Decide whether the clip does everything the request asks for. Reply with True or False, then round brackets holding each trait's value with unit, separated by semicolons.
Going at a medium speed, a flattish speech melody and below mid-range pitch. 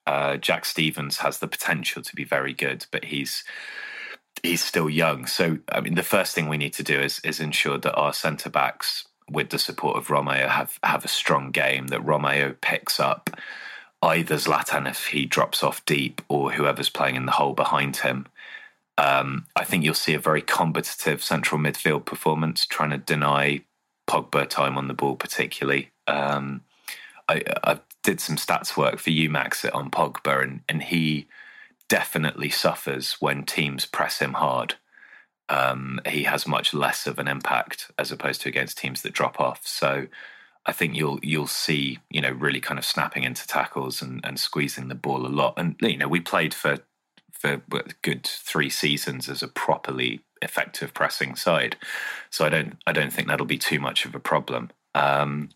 True (185 wpm; 1.8 semitones; 70 Hz)